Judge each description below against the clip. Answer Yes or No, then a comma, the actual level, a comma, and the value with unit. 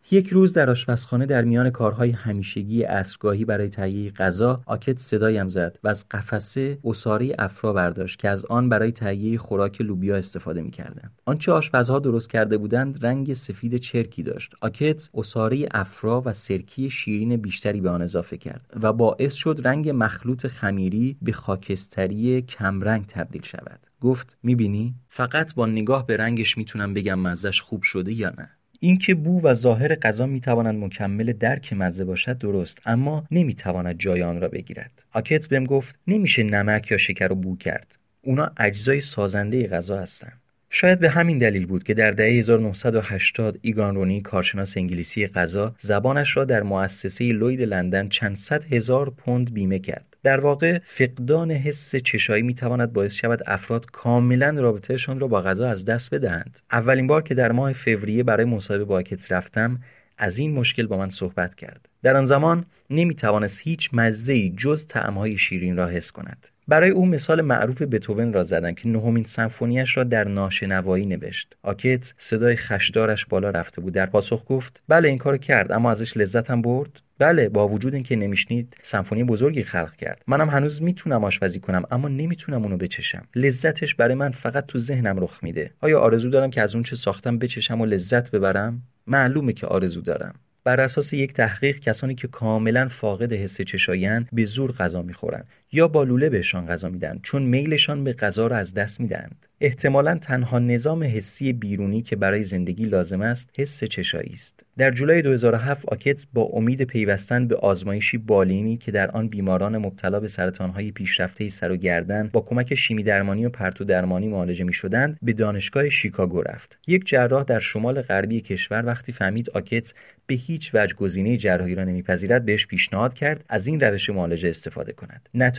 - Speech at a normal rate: No, fast, 170 wpm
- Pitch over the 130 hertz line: No, low, 115 Hz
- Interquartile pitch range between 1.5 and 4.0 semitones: No, average, 4.6 semitones